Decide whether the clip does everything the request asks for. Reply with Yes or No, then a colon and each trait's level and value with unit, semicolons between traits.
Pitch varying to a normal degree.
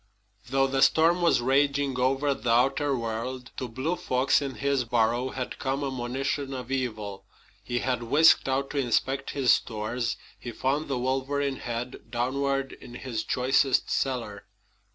No: narrow, 2.2 semitones